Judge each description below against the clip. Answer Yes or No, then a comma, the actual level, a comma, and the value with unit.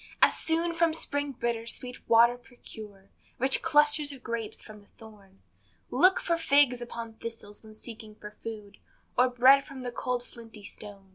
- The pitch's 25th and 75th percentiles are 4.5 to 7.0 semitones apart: No, average, 4.1 semitones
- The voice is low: No, high, 235 Hz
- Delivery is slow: No, average, 165 wpm